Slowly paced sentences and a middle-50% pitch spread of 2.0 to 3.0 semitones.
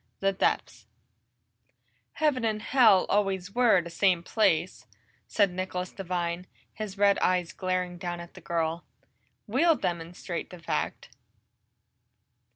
Yes: slow, 125 wpm; average, 2.7 semitones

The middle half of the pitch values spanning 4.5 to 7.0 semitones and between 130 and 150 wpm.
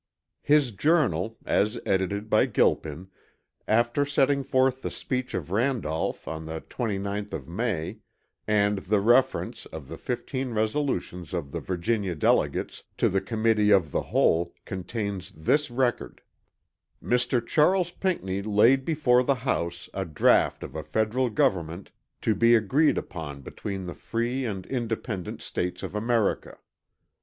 Yes: average, 5.1 semitones; average, 140 wpm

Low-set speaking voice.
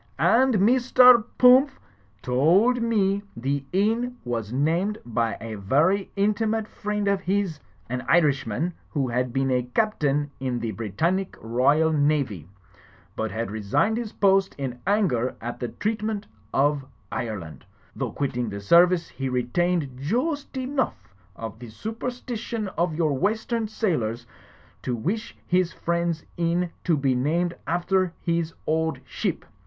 No: medium, 165 Hz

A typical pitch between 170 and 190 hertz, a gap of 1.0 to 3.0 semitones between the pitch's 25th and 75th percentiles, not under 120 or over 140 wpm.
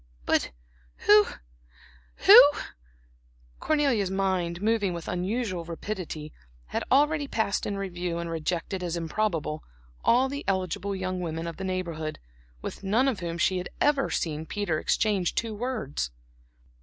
No: medium, 185 Hz; average, 4.1 semitones; slow, 135 wpm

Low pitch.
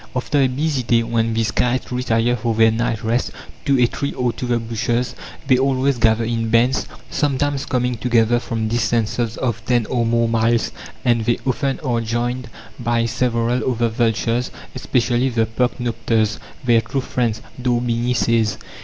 Yes: low, 120 Hz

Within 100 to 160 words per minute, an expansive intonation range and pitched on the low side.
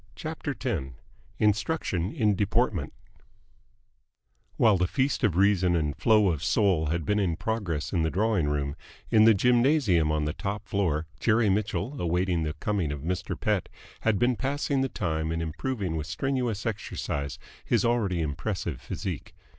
Yes: average, 155 wpm; wide, 5.8 semitones; very low, 95 Hz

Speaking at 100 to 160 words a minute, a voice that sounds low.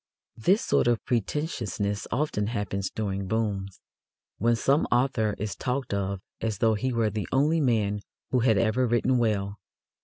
Yes: average, 155 wpm; low, 110 Hz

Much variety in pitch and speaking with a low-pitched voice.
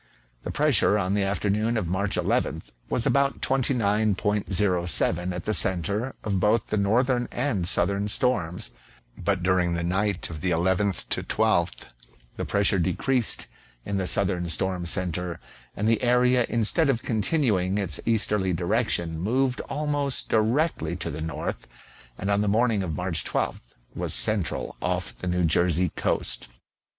No: average, 4.3 semitones; low, 100 Hz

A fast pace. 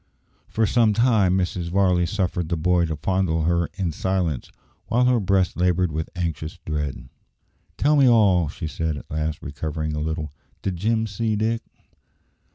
No: average, 165 wpm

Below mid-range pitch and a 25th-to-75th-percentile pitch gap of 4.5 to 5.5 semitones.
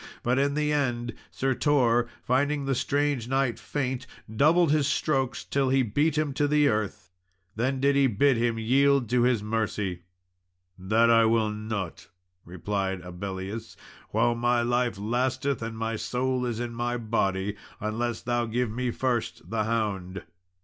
No: low, 120 Hz; average, 3.6 semitones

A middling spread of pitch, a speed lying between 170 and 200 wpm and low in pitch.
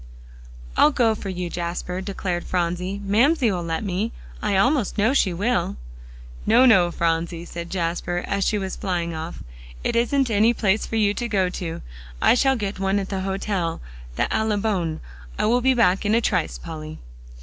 No: average, 4.1 semitones; average, 175 wpm; high, 195 Hz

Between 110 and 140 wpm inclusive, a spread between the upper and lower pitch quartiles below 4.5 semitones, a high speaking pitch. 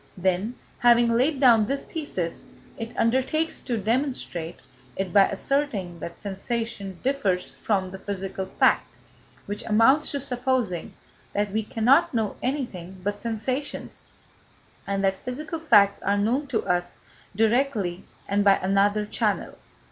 No: slow, 135 wpm; average, 4.8 semitones; high, 215 Hz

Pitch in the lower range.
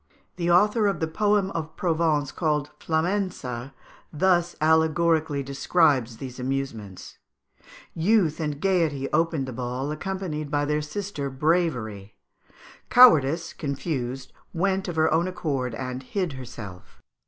No: medium, 155 Hz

